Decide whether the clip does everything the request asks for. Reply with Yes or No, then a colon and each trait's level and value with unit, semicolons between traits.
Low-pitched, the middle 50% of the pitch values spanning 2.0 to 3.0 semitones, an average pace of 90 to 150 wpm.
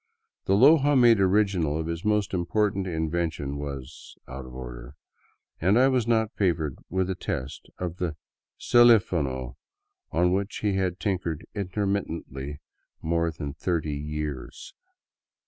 No: very low, 90 Hz; wide, 5.4 semitones; average, 145 wpm